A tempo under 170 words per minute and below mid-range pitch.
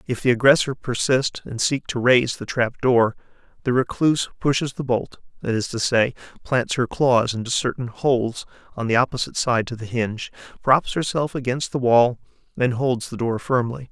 No: average, 185 wpm; low, 125 Hz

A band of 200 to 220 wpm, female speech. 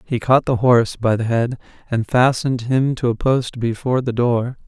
No: fast, 205 wpm; male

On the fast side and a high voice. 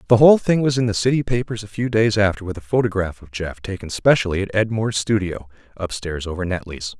No: fast, 225 wpm; low, 105 Hz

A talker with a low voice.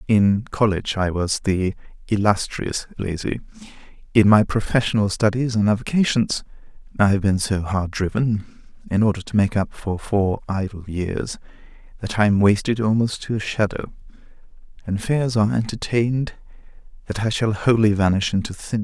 Yes: low, 105 Hz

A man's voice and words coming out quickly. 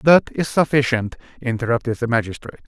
No: male; slow, 135 wpm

